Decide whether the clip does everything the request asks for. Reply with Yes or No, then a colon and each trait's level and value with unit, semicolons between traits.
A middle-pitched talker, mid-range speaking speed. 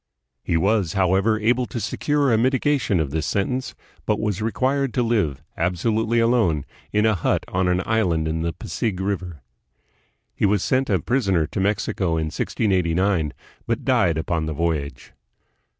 No: very low, 95 Hz; average, 165 wpm